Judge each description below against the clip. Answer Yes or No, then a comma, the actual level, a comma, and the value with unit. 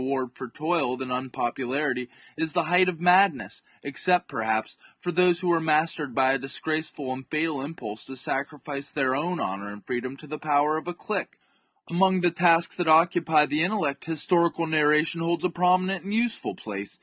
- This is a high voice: No, medium, 155 Hz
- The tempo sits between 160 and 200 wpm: Yes, average, 185 wpm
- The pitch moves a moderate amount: Yes, average, 4.6 semitones